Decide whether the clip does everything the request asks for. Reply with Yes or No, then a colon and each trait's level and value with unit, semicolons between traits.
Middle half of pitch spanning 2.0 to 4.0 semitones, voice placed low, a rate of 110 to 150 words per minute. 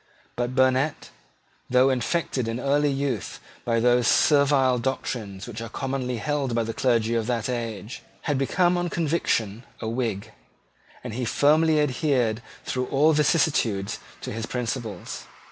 Yes: average, 3.6 semitones; low, 125 Hz; average, 145 wpm